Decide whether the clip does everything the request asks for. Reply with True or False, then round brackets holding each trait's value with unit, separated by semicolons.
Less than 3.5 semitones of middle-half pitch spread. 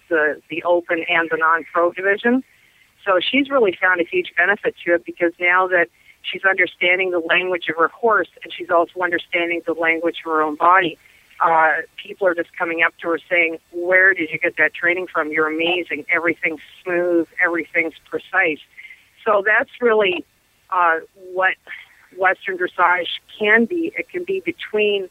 True (2.5 semitones)